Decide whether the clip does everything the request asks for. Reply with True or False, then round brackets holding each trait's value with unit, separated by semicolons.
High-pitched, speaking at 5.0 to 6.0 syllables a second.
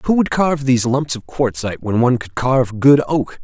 False (130 Hz; 5.9 syllables/s)